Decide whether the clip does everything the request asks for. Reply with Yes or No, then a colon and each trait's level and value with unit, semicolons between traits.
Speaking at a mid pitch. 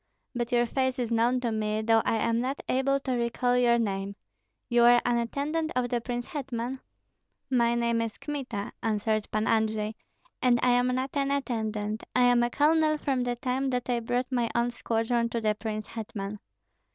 No: high, 240 Hz